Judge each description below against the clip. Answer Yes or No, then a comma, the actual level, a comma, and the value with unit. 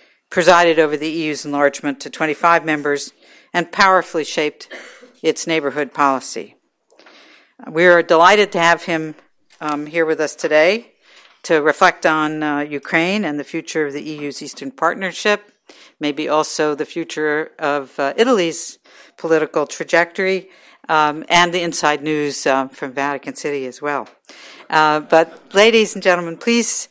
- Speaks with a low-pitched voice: No, medium, 160 Hz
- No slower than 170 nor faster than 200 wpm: No, average, 145 wpm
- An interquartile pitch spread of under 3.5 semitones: Yes, average, 2.9 semitones